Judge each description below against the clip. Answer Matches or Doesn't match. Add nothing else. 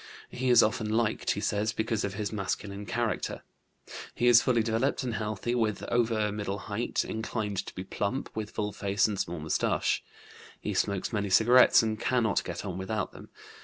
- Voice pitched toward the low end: Matches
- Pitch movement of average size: Doesn't match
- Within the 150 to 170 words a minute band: Doesn't match